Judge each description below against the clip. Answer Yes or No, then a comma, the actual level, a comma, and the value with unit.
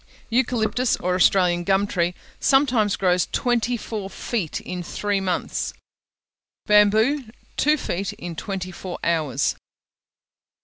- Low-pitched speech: No, high, 200 Hz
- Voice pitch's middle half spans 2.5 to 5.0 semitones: Yes, average, 4.5 semitones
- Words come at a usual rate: No, slow, 115 wpm